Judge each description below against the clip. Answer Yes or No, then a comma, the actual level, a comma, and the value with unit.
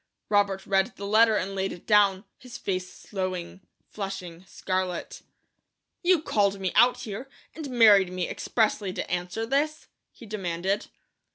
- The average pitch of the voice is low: No, high, 200 Hz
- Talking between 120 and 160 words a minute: Yes, average, 145 wpm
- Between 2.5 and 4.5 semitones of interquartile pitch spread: Yes, average, 3.2 semitones